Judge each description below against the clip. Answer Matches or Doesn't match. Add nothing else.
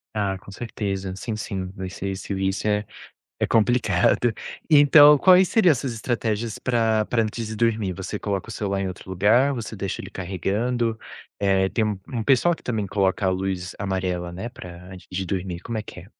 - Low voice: Matches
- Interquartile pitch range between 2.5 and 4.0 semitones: Matches